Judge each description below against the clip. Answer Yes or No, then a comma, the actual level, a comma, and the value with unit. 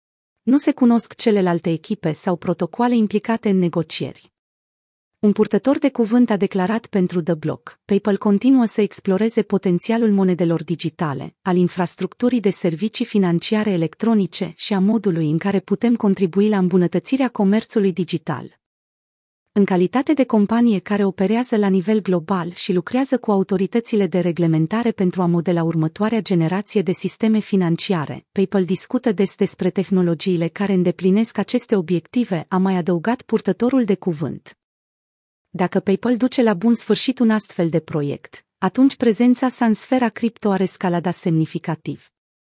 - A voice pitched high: Yes, high, 195 Hz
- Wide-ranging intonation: No, average, 3.7 semitones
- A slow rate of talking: No, average, 140 wpm